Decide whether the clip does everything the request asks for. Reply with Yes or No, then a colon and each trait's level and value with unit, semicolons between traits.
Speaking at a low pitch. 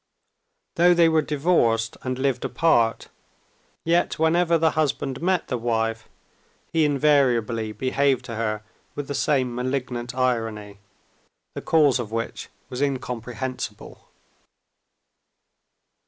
Yes: low, 130 Hz